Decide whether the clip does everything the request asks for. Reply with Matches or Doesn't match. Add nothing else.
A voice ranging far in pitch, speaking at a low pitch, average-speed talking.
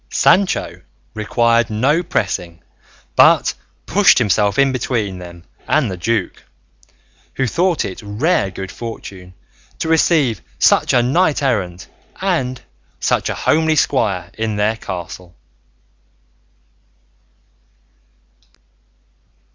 Doesn't match